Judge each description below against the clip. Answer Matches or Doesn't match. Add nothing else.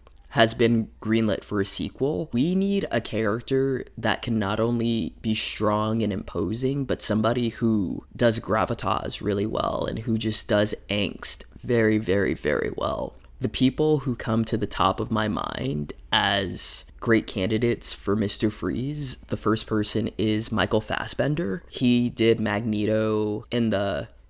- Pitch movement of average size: Doesn't match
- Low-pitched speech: Matches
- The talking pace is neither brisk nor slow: Matches